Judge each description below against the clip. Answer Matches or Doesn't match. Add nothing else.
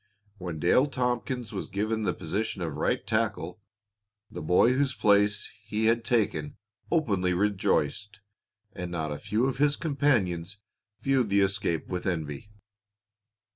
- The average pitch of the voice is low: Matches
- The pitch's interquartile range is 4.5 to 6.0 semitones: Matches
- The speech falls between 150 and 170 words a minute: Doesn't match